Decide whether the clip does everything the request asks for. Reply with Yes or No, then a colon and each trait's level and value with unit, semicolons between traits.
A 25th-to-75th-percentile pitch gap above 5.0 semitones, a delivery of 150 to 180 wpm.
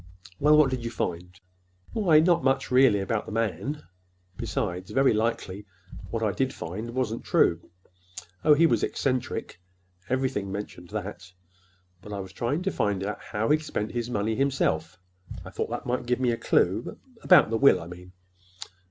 Yes: wide, 5.5 semitones; average, 170 wpm